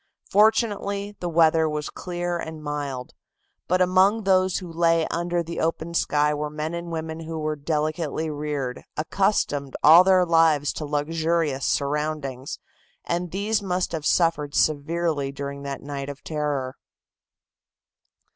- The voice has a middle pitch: Yes, medium, 160 Hz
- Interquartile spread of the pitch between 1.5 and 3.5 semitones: Yes, average, 2.9 semitones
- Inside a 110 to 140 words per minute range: Yes, slow, 135 wpm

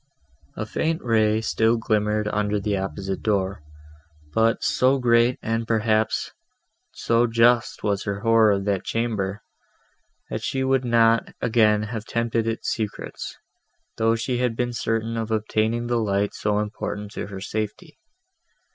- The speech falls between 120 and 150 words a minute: Yes, average, 145 wpm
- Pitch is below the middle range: Yes, low, 110 Hz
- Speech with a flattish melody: Yes, narrow, 1.9 semitones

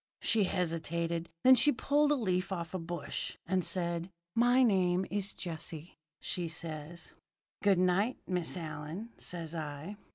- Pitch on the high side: No, medium, 180 Hz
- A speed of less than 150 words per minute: Yes, average, 140 wpm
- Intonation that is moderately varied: Yes, average, 3.3 semitones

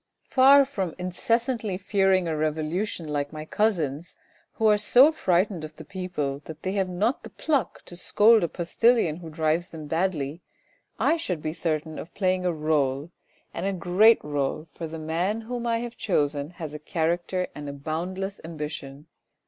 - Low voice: No, medium, 175 Hz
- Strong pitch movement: No, average, 4.4 semitones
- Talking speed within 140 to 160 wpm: No, average, 175 wpm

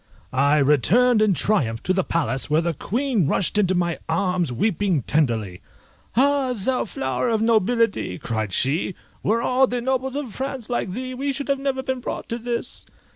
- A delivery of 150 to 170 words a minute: No, average, 180 wpm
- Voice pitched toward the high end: Yes, high, 210 Hz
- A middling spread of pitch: No, wide, 8.4 semitones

